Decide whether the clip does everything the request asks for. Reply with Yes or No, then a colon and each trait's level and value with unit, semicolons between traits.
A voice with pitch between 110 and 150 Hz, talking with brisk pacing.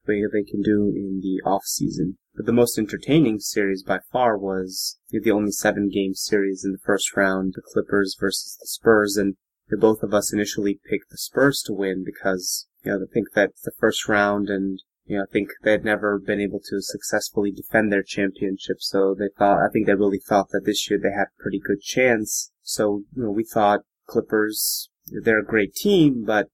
No: low, 100 Hz; fast, 210 wpm